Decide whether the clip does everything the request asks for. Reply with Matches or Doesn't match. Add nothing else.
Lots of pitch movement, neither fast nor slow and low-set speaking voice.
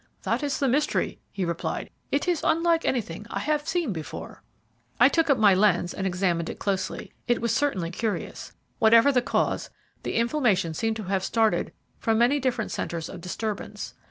Doesn't match